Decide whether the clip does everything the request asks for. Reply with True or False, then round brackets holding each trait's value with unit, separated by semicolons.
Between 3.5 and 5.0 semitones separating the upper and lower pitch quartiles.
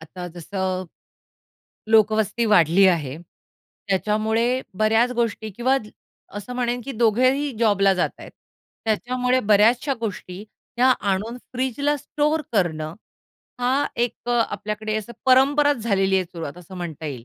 True (4.6 semitones)